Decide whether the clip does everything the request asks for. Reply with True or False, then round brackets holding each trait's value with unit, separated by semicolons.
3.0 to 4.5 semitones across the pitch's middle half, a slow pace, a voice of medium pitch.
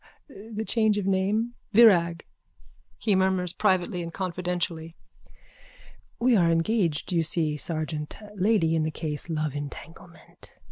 True (3.9 semitones; 125 wpm; 175 Hz)